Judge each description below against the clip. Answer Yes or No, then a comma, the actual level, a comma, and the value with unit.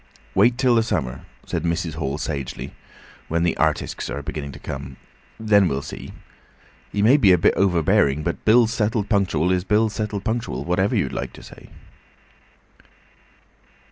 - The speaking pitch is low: Yes, very low, 90 Hz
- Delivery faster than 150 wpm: Yes, average, 160 wpm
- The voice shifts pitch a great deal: Yes, wide, 6.0 semitones